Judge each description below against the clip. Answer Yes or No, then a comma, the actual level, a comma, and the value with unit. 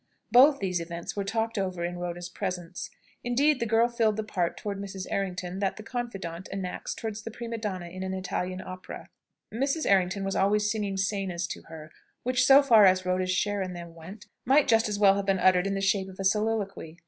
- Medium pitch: No, high, 195 Hz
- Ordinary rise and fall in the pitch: Yes, average, 3.3 semitones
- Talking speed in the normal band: No, fast, 210 wpm